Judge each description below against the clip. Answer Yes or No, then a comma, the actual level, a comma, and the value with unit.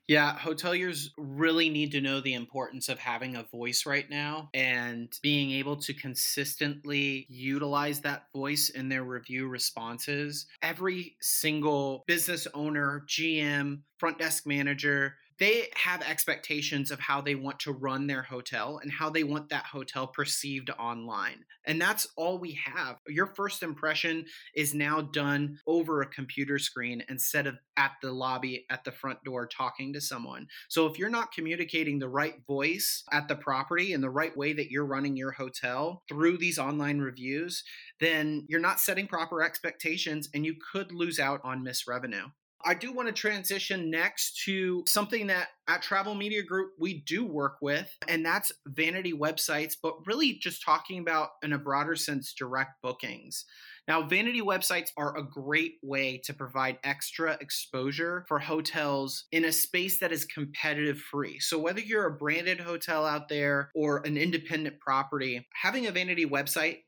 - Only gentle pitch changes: No, average, 3.1 semitones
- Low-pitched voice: No, medium, 150 Hz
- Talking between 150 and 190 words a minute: Yes, average, 165 wpm